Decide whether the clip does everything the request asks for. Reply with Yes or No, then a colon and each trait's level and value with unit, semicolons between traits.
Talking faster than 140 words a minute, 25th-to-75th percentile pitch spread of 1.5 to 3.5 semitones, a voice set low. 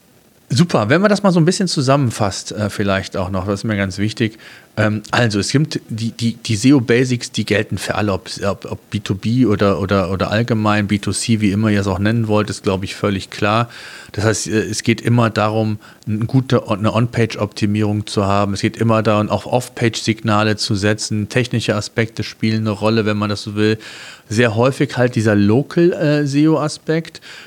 Yes: average, 180 wpm; average, 2.7 semitones; low, 110 Hz